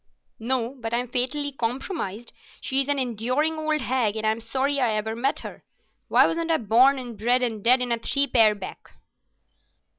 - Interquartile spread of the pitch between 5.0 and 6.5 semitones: No, average, 3.3 semitones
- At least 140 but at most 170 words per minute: No, average, 180 wpm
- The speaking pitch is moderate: No, very high, 250 Hz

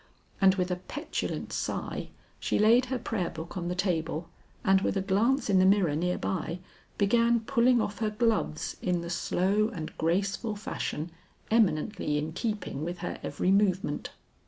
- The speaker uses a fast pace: No, average, 165 wpm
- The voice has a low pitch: No, high, 195 Hz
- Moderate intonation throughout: Yes, average, 4.0 semitones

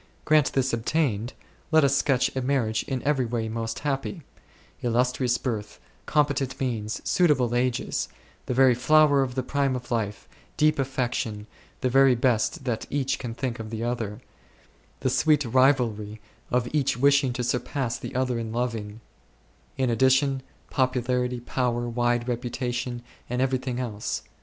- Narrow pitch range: Yes, narrow, 2.2 semitones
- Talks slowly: No, average, 150 wpm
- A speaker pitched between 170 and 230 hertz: No, low, 125 Hz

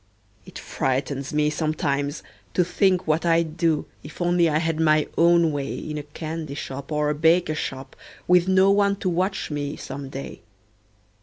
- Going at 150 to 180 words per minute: Yes, average, 170 wpm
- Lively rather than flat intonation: No, average, 2.9 semitones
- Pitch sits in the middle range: Yes, medium, 155 Hz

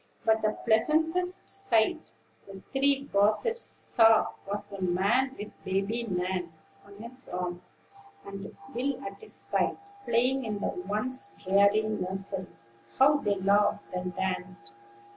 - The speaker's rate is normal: No, slow, 130 wpm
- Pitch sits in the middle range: No, high, 210 Hz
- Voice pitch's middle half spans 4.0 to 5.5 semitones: Yes, average, 4.9 semitones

